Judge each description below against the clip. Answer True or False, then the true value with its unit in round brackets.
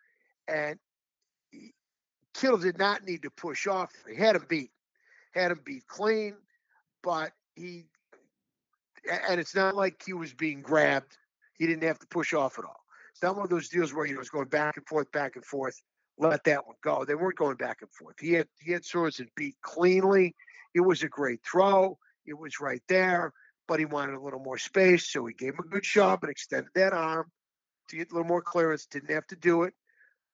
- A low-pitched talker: False (175 Hz)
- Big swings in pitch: False (4.0 semitones)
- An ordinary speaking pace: False (210 wpm)